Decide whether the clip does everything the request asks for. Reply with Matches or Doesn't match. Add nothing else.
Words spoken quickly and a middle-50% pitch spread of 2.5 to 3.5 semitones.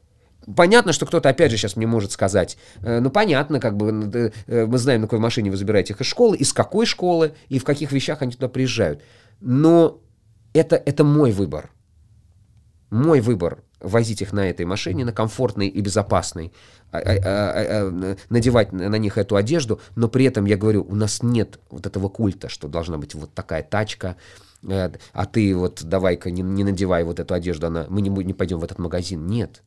Doesn't match